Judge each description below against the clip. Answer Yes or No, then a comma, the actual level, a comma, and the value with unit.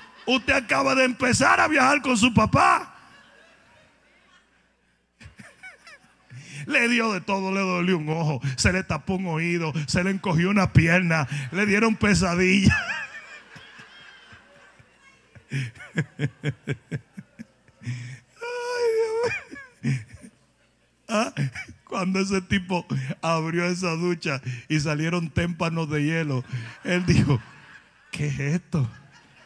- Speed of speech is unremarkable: No, slow, 95 wpm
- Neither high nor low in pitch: Yes, medium, 165 Hz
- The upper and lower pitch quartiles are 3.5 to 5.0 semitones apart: No, wide, 5.6 semitones